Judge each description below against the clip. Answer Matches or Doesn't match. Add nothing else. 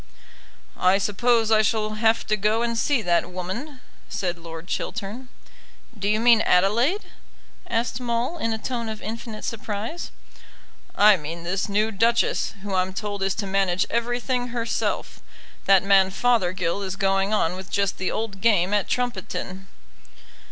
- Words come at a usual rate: Matches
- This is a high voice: Matches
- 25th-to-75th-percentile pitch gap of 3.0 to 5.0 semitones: Matches